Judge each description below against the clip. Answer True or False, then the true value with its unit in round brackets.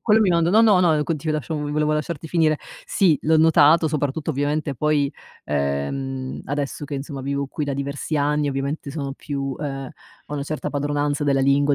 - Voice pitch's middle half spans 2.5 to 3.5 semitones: False (1.9 semitones)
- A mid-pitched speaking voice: True (145 Hz)